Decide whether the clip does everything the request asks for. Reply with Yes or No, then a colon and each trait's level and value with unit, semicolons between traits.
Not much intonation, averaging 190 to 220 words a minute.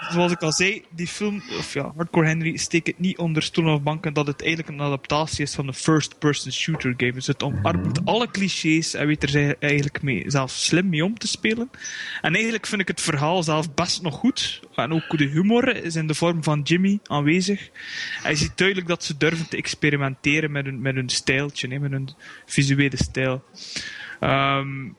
No: average, 3.7 semitones; average, 195 wpm